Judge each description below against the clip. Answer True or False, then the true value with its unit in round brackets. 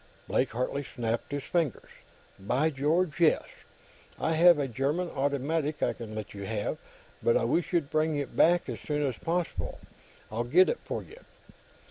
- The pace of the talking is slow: False (170 wpm)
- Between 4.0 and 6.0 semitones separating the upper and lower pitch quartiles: True (4.9 semitones)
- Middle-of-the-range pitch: True (145 Hz)